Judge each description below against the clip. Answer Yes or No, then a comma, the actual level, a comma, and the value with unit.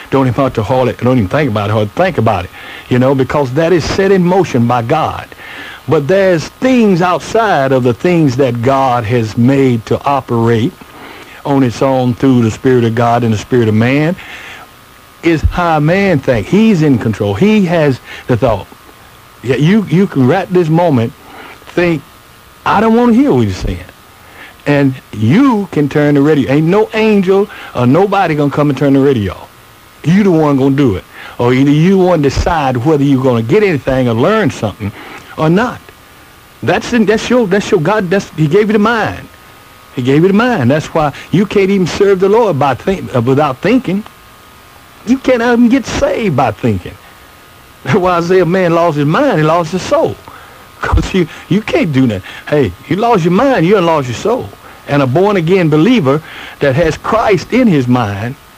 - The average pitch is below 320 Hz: Yes, medium, 140 Hz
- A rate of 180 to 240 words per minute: Yes, average, 200 wpm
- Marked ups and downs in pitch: Yes, wide, 7.6 semitones